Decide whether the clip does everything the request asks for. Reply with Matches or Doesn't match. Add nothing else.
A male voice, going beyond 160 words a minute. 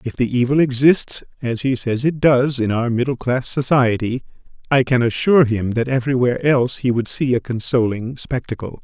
Matches